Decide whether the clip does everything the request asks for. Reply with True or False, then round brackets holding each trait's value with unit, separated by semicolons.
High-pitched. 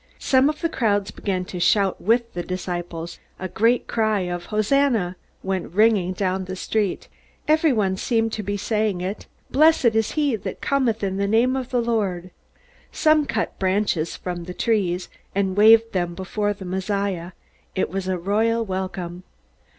True (200 Hz)